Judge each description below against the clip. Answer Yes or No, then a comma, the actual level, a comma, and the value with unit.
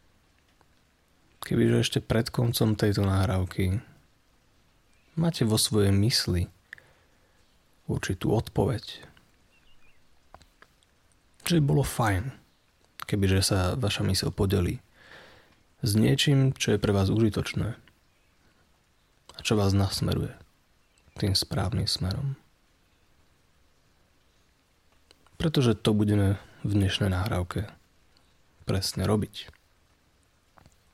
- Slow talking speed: Yes, slow, 85 wpm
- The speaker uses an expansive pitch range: No, average, 4.0 semitones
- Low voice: Yes, low, 100 Hz